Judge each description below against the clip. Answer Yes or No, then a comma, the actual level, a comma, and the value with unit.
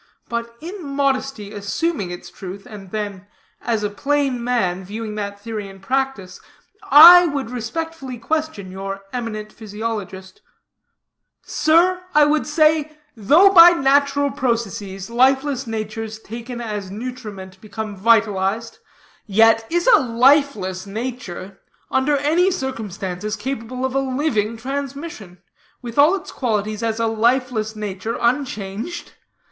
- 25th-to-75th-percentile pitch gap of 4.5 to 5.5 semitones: Yes, average, 5.1 semitones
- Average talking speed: No, slow, 125 wpm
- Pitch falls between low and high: No, high, 230 Hz